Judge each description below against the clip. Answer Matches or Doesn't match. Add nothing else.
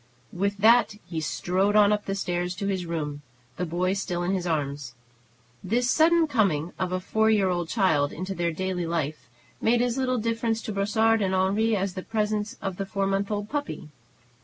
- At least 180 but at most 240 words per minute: Matches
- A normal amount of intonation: Matches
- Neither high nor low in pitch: Doesn't match